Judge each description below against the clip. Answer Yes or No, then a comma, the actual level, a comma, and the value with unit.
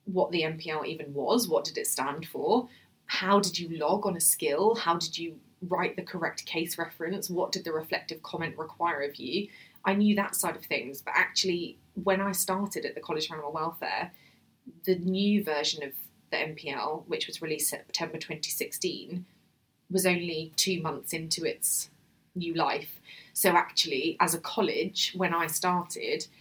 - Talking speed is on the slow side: No, average, 175 wpm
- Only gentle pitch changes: No, average, 3.2 semitones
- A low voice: No, medium, 170 Hz